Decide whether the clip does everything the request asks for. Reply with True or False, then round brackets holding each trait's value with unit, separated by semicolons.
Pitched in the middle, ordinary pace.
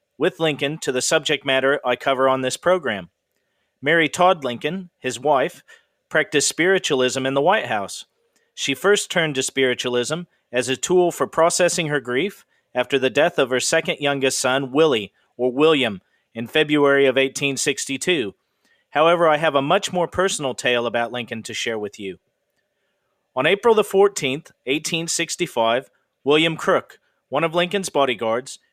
True (145 Hz; 160 wpm)